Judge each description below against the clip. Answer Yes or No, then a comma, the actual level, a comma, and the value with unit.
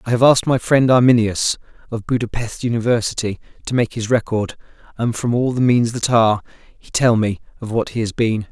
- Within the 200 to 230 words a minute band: Yes, fast, 205 wpm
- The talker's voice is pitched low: Yes, low, 115 Hz